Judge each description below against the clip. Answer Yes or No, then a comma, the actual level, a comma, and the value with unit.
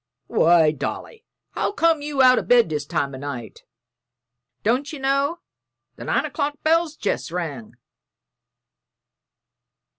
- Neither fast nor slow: No, slow, 125 wpm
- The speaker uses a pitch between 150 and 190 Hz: No, very high, 255 Hz